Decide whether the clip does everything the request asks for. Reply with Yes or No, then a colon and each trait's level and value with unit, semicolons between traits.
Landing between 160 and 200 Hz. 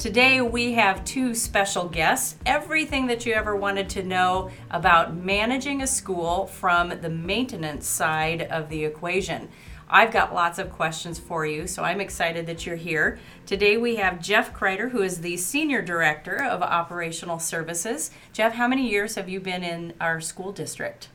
Yes: medium, 185 Hz